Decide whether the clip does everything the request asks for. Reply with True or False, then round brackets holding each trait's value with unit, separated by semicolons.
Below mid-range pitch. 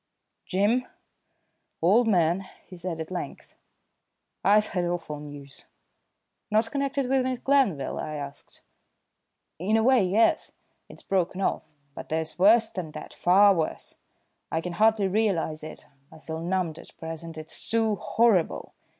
False (185 Hz)